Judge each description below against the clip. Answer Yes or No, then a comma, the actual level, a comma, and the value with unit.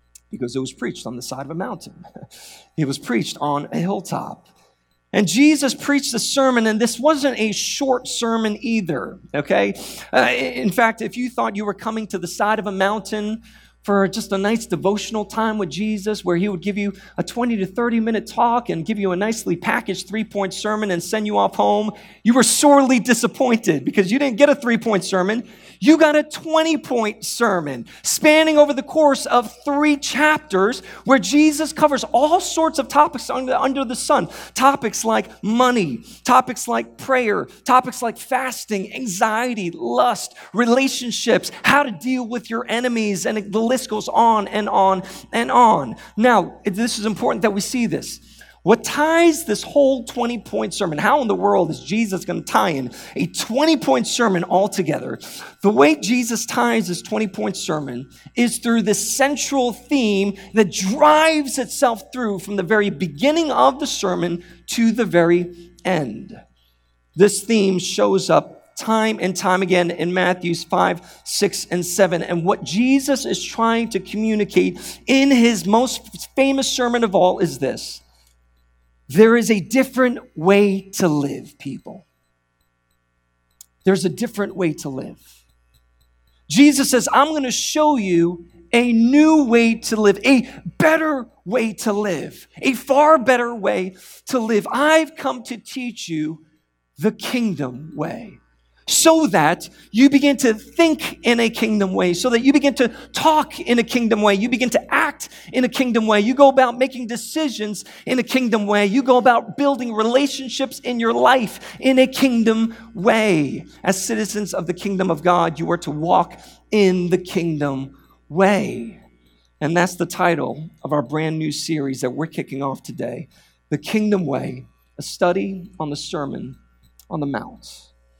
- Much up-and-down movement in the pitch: Yes, wide, 5.9 semitones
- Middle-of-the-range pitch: No, high, 215 Hz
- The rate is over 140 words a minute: Yes, average, 170 wpm